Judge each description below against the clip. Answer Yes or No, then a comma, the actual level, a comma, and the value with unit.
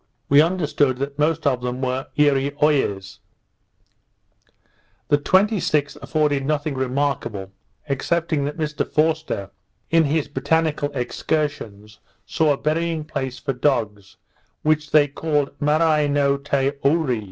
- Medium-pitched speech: Yes, medium, 145 Hz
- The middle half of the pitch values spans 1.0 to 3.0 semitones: Yes, narrow, 2.5 semitones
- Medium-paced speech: No, slow, 120 wpm